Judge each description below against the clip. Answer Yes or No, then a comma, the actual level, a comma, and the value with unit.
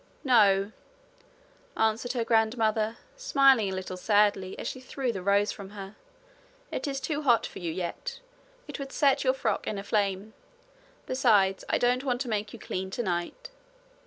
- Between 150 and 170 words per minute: Yes, average, 165 wpm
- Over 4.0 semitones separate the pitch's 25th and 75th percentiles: Yes, average, 4.7 semitones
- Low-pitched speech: No, high, 220 Hz